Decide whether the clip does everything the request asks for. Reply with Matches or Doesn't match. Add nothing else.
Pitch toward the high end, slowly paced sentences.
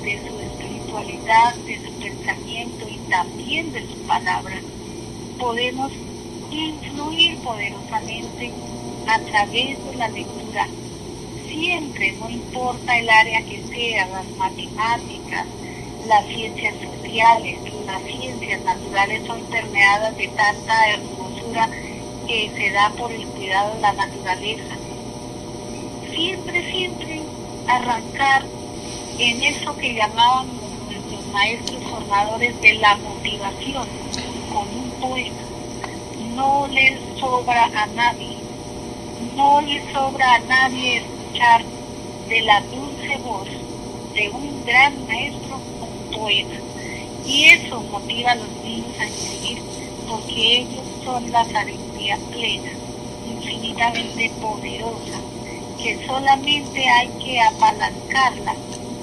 Matches